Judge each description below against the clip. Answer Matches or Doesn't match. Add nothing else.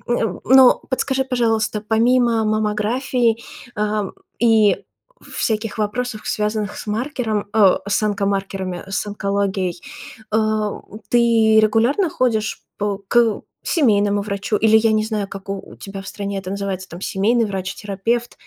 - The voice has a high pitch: Matches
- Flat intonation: Matches